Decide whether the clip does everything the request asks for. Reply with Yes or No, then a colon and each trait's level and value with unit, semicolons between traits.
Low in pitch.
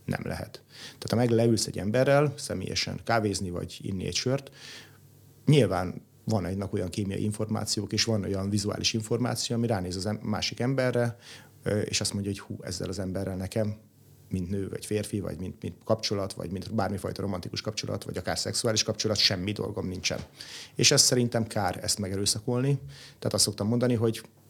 Yes: low, 110 Hz